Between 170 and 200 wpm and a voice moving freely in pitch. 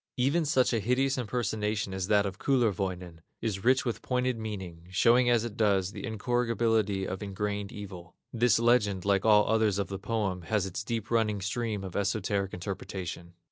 No: average, 175 wpm; average, 3.3 semitones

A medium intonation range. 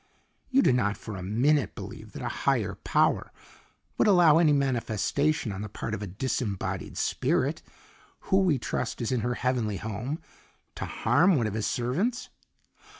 No: wide, 6.1 semitones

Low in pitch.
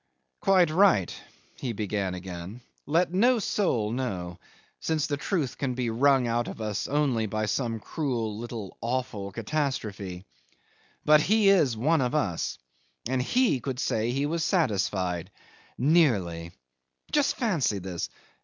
Yes: low, 125 Hz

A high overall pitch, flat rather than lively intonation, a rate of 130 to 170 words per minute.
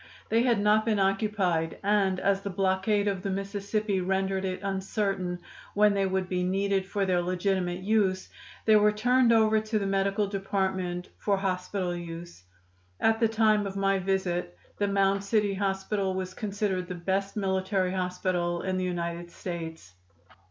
Yes: high, 195 Hz; narrow, 1.8 semitones; average, 160 wpm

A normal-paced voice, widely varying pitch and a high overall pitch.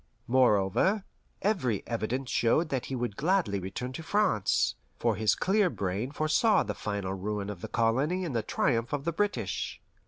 No: average, 165 wpm; wide, 7.6 semitones; low, 125 Hz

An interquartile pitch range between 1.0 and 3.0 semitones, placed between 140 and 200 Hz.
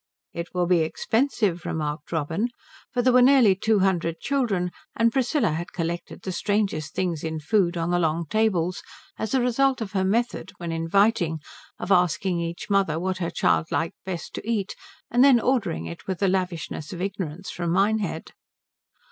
No: average, 4.6 semitones; medium, 185 Hz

